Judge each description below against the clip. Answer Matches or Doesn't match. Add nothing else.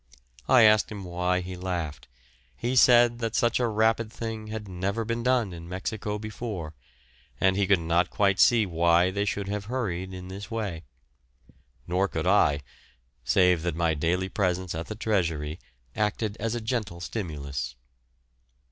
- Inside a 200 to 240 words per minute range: Doesn't match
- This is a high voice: Doesn't match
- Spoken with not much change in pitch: Doesn't match